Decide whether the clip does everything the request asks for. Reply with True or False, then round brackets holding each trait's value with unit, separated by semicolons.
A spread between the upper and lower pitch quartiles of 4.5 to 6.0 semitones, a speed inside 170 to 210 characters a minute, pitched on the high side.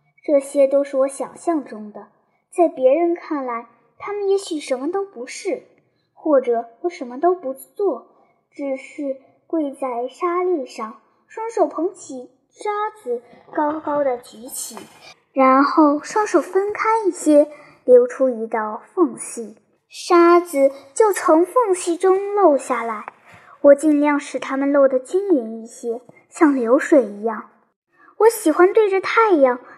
True (5.6 semitones; 195 characters per minute; 290 Hz)